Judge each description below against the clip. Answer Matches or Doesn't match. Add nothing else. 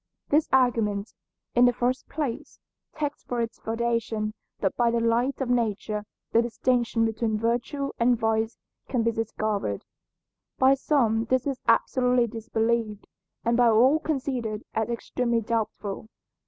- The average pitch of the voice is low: Doesn't match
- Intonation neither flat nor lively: Doesn't match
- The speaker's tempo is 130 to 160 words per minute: Matches